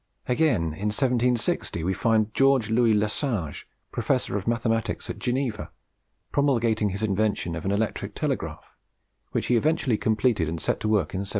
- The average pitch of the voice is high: No, low, 110 Hz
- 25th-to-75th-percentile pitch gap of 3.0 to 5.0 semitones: Yes, average, 3.4 semitones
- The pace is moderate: Yes, average, 160 wpm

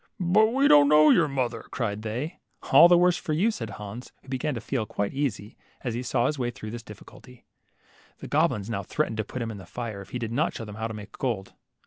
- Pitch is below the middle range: Yes, low, 120 Hz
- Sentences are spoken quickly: Yes, fast, 250 wpm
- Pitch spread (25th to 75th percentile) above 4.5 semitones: Yes, wide, 5.4 semitones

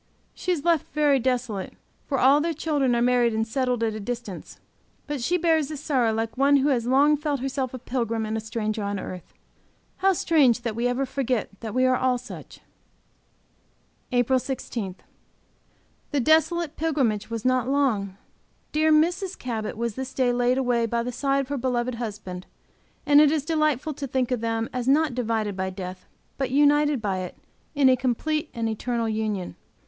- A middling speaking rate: Yes, average, 185 wpm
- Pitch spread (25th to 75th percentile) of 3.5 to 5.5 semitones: Yes, average, 4.0 semitones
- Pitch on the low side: No, very high, 250 Hz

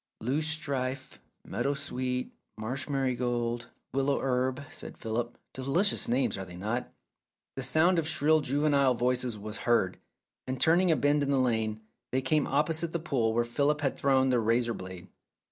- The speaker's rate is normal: Yes, average, 160 wpm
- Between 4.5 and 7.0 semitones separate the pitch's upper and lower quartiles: No, average, 3.2 semitones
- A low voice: Yes, low, 130 Hz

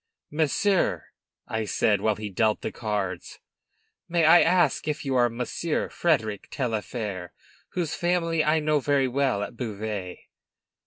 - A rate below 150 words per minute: Yes, average, 140 wpm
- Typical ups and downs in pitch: No, wide, 6.5 semitones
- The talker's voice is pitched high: No, low, 125 Hz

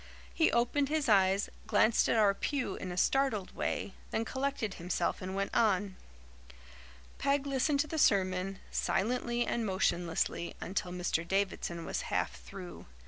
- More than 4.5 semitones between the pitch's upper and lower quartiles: Yes, wide, 5.6 semitones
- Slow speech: No, average, 145 wpm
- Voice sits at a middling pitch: No, high, 200 Hz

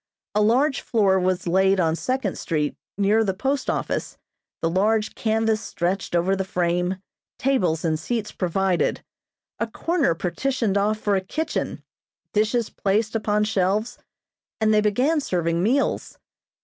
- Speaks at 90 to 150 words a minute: Yes, average, 140 wpm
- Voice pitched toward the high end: Yes, high, 205 Hz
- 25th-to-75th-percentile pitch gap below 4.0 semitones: Yes, average, 3.5 semitones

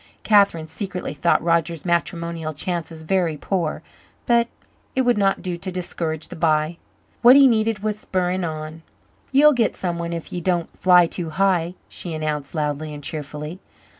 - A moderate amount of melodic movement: Yes, average, 3.5 semitones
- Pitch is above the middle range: No, medium, 170 Hz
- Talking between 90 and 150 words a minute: No, average, 160 wpm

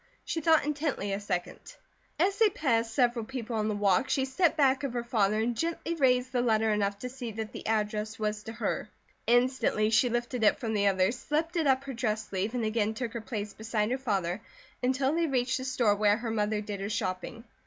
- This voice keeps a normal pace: No, fast, 220 wpm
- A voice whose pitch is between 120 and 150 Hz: No, high, 230 Hz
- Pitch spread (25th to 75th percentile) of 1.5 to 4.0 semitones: Yes, average, 3.7 semitones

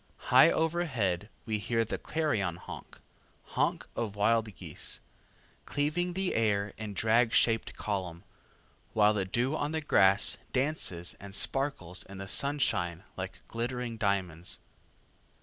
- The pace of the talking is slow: Yes, slow, 130 wpm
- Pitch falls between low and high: No, low, 110 Hz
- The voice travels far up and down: Yes, wide, 5.7 semitones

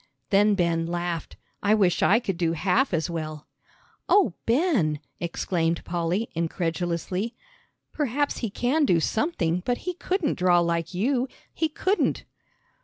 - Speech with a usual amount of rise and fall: No, wide, 6.5 semitones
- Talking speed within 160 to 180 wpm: No, slow, 135 wpm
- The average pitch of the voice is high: No, medium, 180 Hz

